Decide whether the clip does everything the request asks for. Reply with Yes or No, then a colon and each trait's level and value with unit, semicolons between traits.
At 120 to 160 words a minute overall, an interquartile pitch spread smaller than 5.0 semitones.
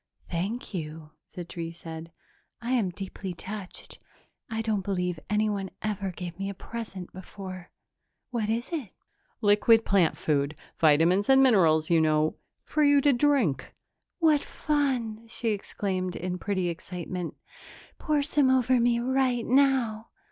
No: average, 140 wpm; average, 5.3 semitones